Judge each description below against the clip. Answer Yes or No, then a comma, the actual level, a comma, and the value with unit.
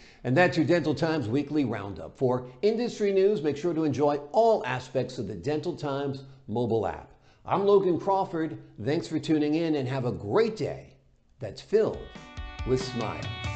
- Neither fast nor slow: Yes, average, 170 wpm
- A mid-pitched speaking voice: Yes, medium, 145 Hz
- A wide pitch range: No, average, 4.8 semitones